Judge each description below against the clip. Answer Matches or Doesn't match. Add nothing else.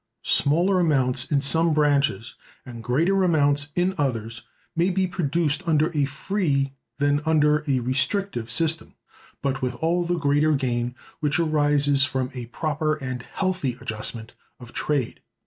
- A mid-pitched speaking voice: Matches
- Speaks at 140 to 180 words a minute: Matches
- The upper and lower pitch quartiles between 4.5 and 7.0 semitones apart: Doesn't match